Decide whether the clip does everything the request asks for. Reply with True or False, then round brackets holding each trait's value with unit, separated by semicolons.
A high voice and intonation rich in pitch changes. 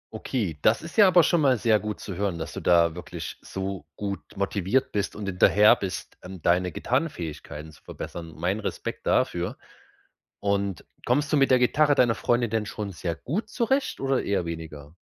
False (100 Hz; 6.5 semitones)